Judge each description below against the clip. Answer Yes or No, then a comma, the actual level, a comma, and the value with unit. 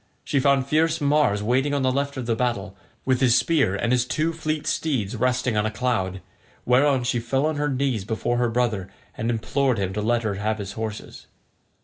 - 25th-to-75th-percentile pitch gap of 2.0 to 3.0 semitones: No, average, 4.2 semitones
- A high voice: No, low, 125 Hz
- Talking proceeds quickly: Yes, fast, 210 wpm